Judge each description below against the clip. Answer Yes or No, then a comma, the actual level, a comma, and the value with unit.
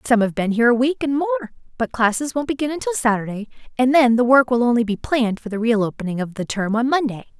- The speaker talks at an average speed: No, fast, 250 wpm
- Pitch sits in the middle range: No, high, 240 Hz